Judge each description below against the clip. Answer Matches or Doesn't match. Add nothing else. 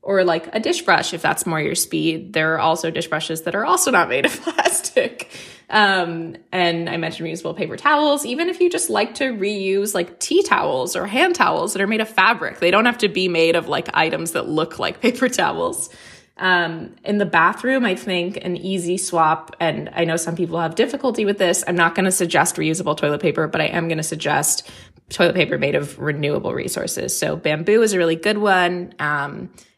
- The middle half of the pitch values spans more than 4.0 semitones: Matches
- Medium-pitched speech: Matches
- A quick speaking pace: Matches